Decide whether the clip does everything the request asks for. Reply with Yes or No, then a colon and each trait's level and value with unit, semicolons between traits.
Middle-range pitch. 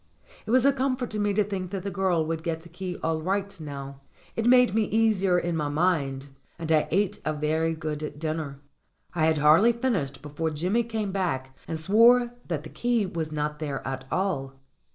Yes: medium, 170 Hz